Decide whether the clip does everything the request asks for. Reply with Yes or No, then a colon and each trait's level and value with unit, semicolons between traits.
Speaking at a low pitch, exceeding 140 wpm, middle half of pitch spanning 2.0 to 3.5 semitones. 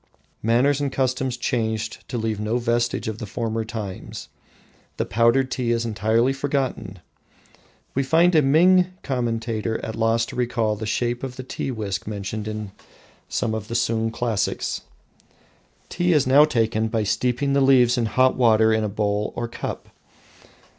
Yes: low, 115 Hz; average, 160 wpm; average, 2.8 semitones